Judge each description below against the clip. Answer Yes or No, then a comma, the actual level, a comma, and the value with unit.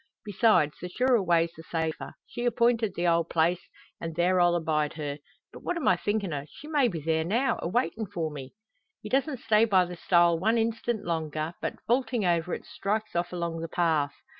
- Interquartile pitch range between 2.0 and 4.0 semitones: No, average, 5.3 semitones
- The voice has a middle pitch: Yes, medium, 175 Hz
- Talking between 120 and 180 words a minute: No, fast, 205 wpm